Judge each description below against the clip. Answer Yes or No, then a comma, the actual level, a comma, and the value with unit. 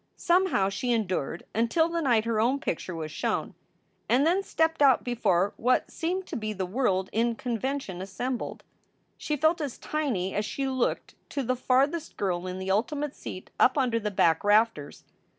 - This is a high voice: Yes, high, 240 Hz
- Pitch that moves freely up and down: Yes, wide, 6.5 semitones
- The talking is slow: No, average, 175 wpm